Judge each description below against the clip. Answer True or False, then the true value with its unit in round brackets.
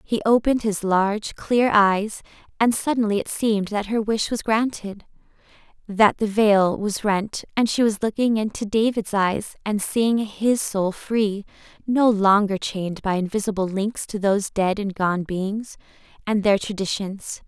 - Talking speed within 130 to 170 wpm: True (160 wpm)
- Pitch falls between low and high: False (210 Hz)